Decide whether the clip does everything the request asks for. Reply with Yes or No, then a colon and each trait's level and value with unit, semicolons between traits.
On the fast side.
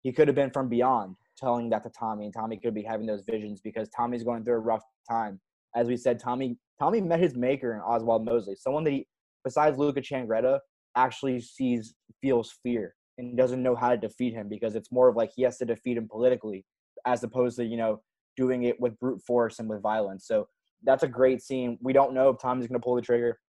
Yes: fast, 230 wpm